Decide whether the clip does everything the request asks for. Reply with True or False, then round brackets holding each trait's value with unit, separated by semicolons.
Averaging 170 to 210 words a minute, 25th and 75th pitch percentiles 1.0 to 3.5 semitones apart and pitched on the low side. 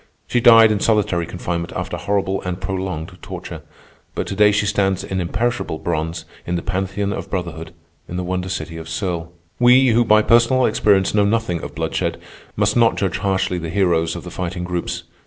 True (190 wpm; 3.2 semitones; 95 Hz)